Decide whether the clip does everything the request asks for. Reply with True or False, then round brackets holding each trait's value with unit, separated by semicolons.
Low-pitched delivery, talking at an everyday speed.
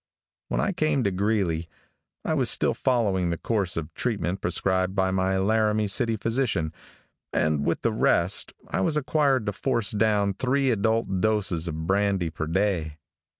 True (100 Hz; 160 wpm)